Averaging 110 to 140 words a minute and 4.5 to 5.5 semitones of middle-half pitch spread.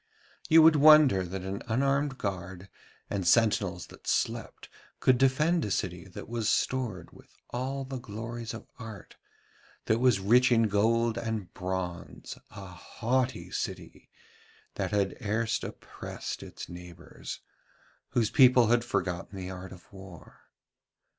Yes: slow, 135 wpm; average, 4.8 semitones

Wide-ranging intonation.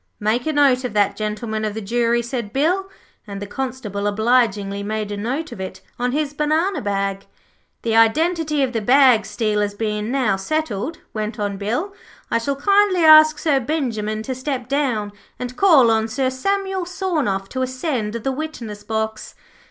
Yes: wide, 5.7 semitones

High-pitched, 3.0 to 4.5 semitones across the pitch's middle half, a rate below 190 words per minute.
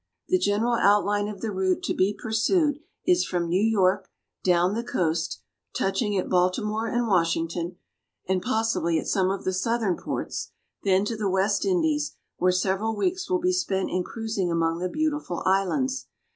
Yes: high, 200 Hz; average, 3.8 semitones; average, 170 wpm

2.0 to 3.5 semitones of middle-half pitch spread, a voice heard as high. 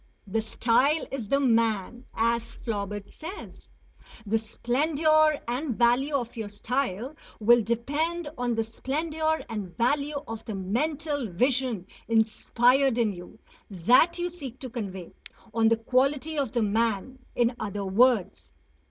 No: average, 4.1 semitones; high, 240 Hz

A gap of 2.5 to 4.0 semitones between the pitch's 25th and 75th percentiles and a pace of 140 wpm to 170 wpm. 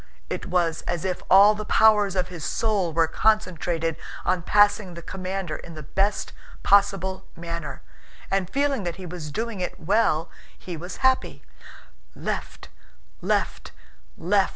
Yes: average, 3.4 semitones; average, 145 wpm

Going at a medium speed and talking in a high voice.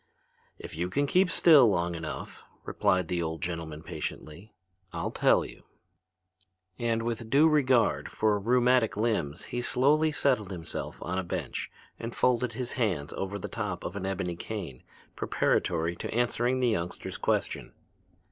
No: average, 150 wpm; low, 110 Hz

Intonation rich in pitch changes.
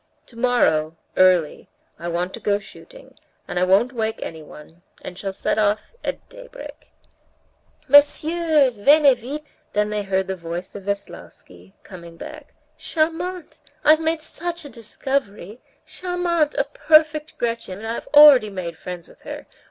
Yes: wide, 8.6 semitones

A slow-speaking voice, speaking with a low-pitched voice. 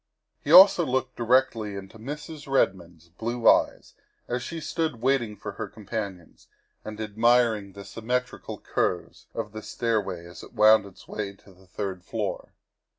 No: average, 150 wpm; low, 110 Hz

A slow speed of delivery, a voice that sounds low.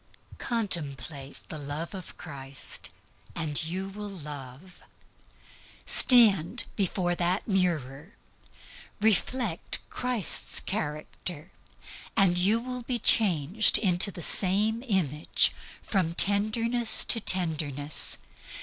No: slow, 95 wpm; medium, 185 Hz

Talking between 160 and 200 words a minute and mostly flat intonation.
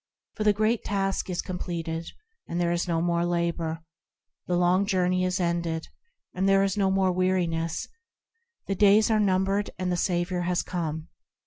Yes: average, 170 wpm; narrow, 2.2 semitones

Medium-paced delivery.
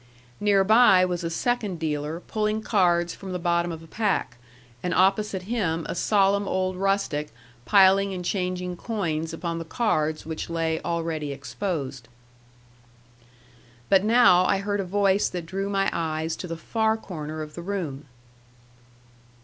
Yes: average, 150 wpm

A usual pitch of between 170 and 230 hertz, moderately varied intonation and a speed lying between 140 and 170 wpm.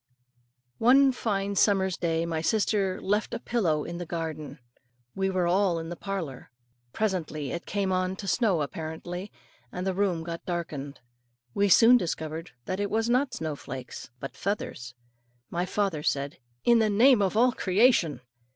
Yes: medium, 185 Hz; average, 4.0 semitones; average, 160 wpm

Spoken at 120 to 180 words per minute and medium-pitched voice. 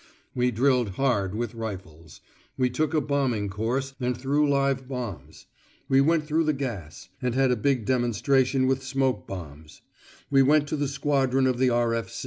No: average, 170 wpm; low, 130 Hz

